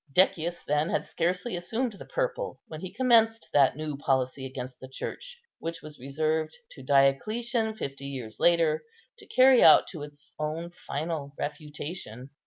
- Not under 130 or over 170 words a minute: Yes, average, 155 wpm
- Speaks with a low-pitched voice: No, medium, 155 Hz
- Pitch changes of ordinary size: No, wide, 7.4 semitones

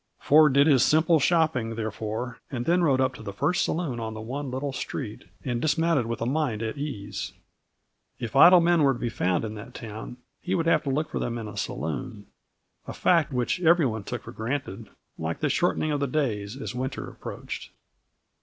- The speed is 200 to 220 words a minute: Yes, fast, 205 wpm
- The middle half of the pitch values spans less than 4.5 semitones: No, average, 5.3 semitones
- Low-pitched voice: Yes, low, 130 Hz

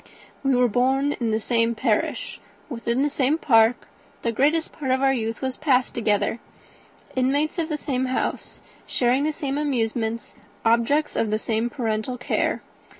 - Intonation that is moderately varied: Yes, average, 3.4 semitones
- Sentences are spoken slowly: No, average, 160 wpm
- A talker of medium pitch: No, very high, 250 Hz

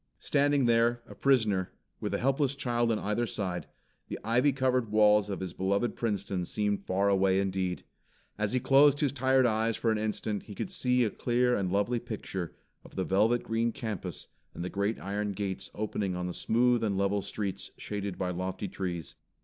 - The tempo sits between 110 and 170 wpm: No, average, 190 wpm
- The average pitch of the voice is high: No, low, 105 Hz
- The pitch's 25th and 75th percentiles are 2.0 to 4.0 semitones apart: Yes, average, 3.7 semitones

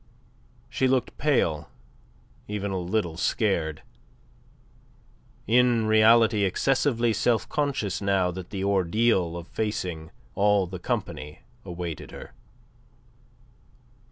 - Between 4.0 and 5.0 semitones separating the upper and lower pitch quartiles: Yes, average, 4.4 semitones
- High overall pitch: No, low, 100 Hz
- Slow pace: Yes, slow, 100 wpm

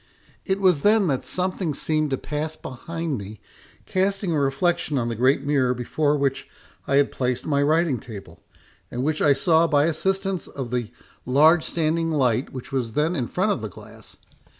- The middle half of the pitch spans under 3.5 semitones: No, average, 4.6 semitones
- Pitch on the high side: No, medium, 145 Hz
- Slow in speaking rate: No, average, 180 wpm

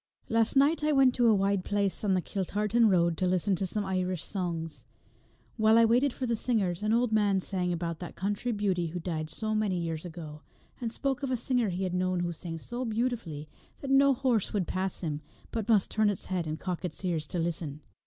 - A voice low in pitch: No, high, 195 Hz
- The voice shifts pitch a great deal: No, average, 4.5 semitones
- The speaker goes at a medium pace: No, fast, 225 wpm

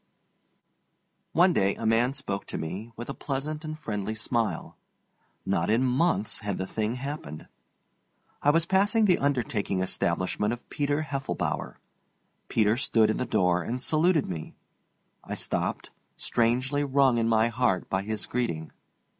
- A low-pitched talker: Yes, low, 120 Hz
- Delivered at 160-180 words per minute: No, average, 145 wpm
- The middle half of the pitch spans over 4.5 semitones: Yes, average, 5.3 semitones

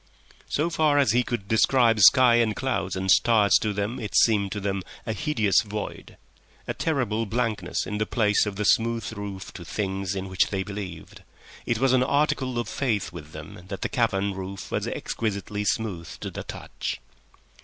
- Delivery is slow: No, average, 180 wpm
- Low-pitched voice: Yes, low, 105 Hz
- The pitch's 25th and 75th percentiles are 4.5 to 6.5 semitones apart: No, average, 3.4 semitones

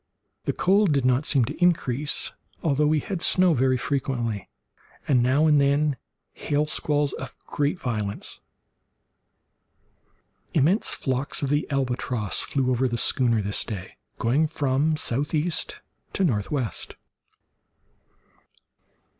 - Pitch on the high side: No, medium, 140 Hz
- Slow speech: Yes, slow, 120 wpm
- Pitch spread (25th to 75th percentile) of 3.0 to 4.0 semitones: Yes, average, 3.4 semitones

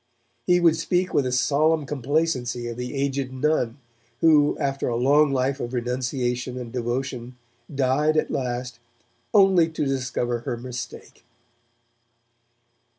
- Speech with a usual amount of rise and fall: Yes, average, 3.4 semitones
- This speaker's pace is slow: Yes, slow, 130 wpm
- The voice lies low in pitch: Yes, low, 130 Hz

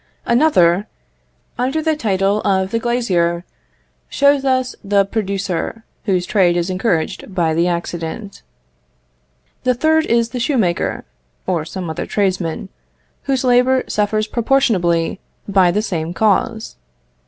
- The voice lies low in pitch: No, high, 200 Hz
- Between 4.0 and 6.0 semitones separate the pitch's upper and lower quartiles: Yes, wide, 5.4 semitones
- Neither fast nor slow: No, slow, 120 wpm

